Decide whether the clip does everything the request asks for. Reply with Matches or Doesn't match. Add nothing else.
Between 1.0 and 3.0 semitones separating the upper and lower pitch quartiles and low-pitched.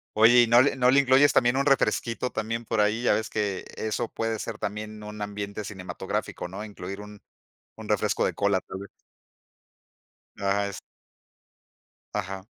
Matches